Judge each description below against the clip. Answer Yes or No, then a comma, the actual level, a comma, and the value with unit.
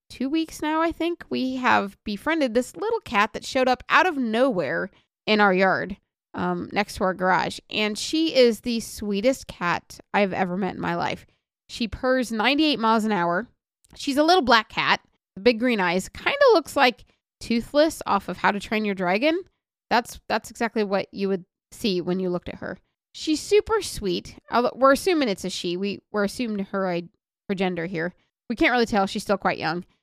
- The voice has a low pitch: No, high, 220 Hz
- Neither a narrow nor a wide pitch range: No, wide, 5.9 semitones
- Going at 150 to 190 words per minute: No, average, 200 wpm